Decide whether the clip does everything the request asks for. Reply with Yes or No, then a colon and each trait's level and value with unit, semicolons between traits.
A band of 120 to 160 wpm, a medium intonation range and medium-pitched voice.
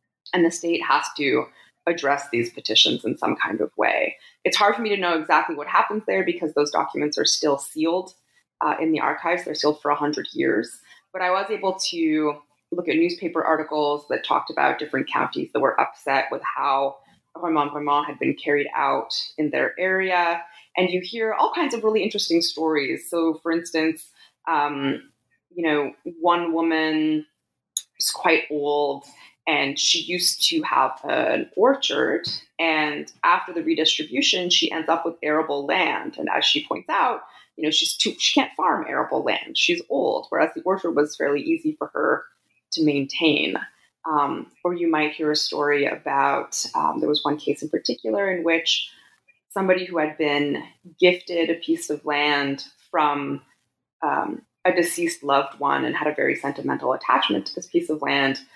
No: average, 175 wpm; average, 3.3 semitones; medium, 160 Hz